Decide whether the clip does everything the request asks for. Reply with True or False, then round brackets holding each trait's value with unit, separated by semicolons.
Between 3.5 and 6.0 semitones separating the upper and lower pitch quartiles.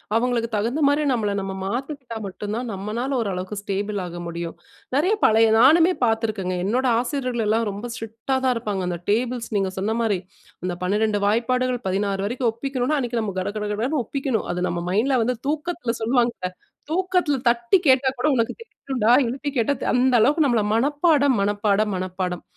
True (4.2 semitones)